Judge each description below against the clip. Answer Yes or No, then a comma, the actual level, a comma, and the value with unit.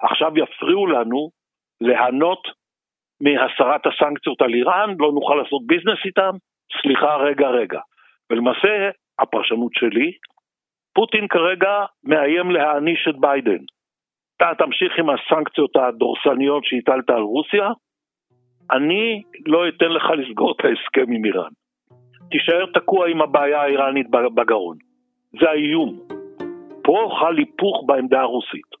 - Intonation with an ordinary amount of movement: No, wide, 7.4 semitones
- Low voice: No, medium, 160 Hz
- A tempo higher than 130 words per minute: No, average, 115 wpm